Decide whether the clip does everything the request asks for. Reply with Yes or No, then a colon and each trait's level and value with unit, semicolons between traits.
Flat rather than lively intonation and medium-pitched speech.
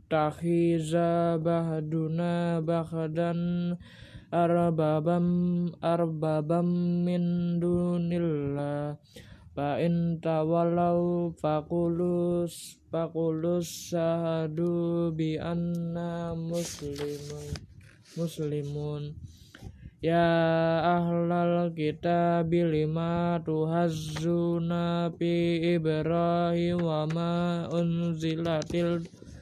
Yes: narrow, 1.3 semitones; medium, 170 Hz